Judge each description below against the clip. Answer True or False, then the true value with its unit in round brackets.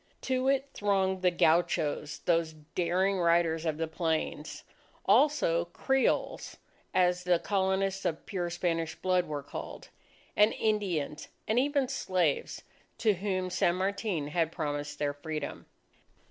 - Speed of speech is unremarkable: False (130 wpm)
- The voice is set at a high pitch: False (180 Hz)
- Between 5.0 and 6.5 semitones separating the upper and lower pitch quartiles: False (3.4 semitones)